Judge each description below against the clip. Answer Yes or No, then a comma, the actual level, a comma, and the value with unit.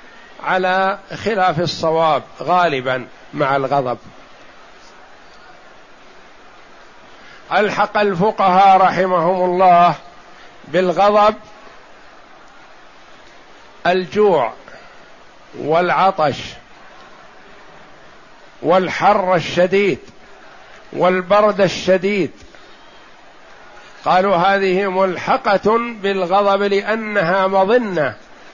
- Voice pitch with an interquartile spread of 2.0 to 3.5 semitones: Yes, narrow, 2.4 semitones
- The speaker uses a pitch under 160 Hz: No, medium, 185 Hz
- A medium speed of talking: No, slow, 50 wpm